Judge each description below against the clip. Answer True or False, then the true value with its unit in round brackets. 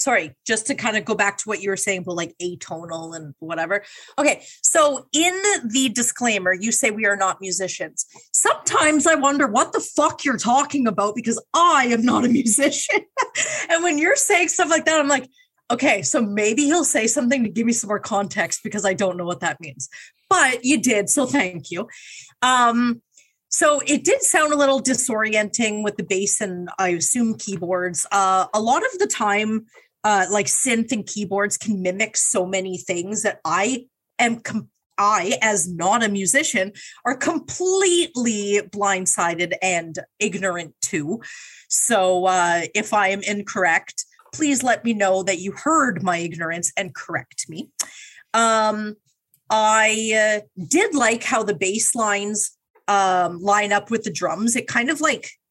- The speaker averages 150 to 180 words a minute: True (175 wpm)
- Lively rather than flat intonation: True (6.0 semitones)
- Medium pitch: False (215 Hz)